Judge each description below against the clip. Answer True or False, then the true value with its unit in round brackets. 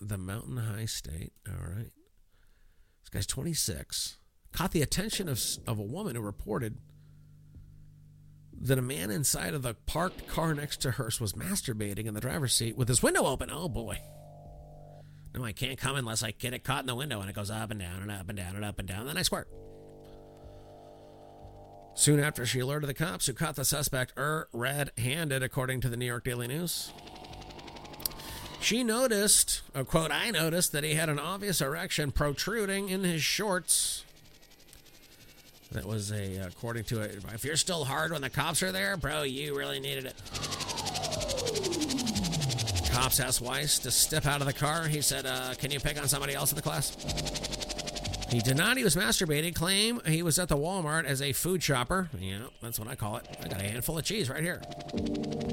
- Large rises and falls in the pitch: True (5.8 semitones)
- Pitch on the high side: False (135 Hz)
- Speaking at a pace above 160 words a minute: True (190 wpm)